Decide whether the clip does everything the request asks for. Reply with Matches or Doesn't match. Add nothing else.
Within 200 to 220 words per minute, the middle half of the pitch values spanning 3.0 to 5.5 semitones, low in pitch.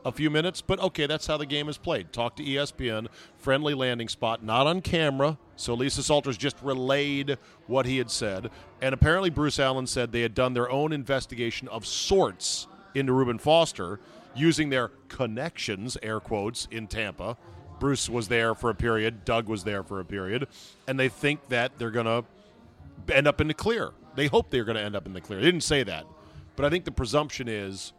Matches